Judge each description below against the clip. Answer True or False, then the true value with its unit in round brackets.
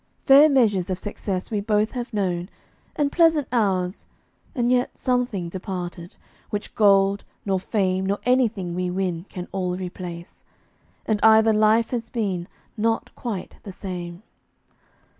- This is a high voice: True (200 Hz)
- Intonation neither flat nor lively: True (3.8 semitones)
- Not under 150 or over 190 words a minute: False (140 wpm)